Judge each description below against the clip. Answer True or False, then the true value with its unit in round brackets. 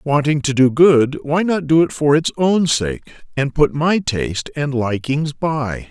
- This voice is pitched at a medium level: True (145 Hz)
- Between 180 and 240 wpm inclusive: True (195 wpm)